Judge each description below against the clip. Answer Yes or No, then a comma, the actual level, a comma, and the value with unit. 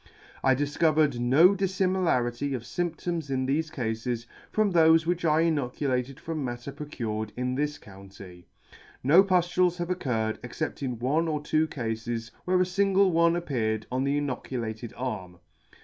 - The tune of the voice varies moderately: No, wide, 5.7 semitones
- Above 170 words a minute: No, average, 150 wpm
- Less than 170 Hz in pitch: Yes, medium, 140 Hz